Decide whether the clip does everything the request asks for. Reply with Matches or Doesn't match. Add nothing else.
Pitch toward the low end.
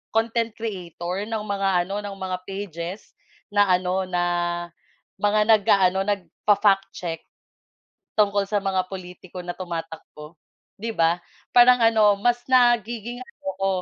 Doesn't match